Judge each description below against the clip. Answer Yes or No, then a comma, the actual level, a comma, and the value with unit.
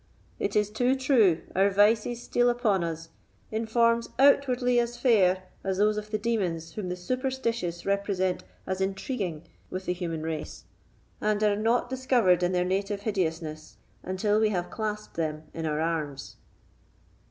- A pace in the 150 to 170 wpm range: Yes, average, 155 wpm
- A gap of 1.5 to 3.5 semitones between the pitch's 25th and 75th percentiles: No, average, 4.6 semitones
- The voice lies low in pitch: No, high, 200 Hz